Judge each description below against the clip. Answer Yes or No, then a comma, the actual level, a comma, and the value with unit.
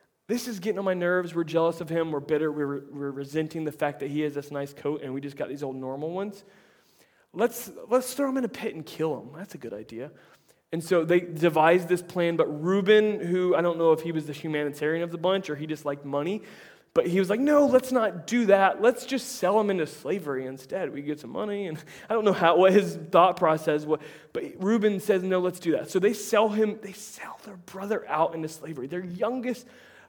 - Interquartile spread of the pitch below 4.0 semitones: No, wide, 5.4 semitones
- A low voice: No, medium, 175 Hz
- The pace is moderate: No, fast, 240 wpm